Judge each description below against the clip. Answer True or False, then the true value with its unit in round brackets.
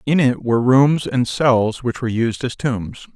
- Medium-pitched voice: False (125 Hz)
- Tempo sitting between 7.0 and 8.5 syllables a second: False (4.4 syllables/s)